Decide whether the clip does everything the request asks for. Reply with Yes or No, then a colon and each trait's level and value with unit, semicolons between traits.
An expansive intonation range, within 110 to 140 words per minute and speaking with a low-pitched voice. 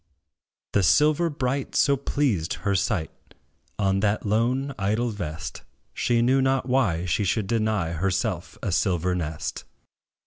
Yes: wide, 5.9 semitones; slow, 135 wpm; low, 105 Hz